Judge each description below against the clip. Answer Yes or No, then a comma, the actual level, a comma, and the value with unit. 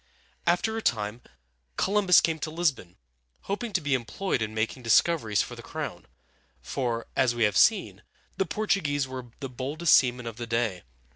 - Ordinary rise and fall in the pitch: No, wide, 6.9 semitones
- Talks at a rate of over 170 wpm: No, average, 165 wpm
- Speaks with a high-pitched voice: No, low, 130 Hz